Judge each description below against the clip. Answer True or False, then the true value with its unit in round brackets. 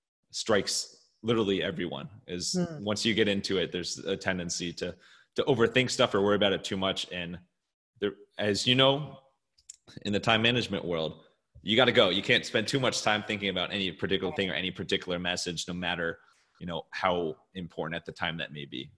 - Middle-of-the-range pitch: False (100 Hz)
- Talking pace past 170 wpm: True (200 wpm)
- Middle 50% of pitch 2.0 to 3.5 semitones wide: False (4.2 semitones)